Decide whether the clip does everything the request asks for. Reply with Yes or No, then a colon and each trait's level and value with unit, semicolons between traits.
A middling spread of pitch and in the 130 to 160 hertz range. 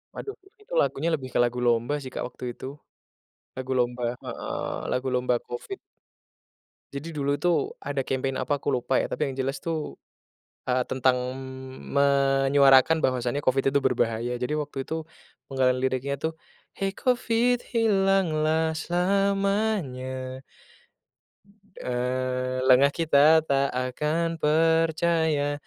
Yes: average, 3.9 semitones; medium, 140 Hz